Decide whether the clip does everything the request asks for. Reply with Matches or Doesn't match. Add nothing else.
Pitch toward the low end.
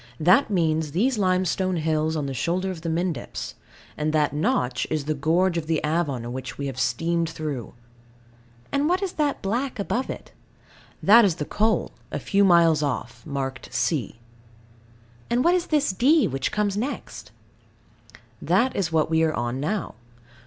Doesn't match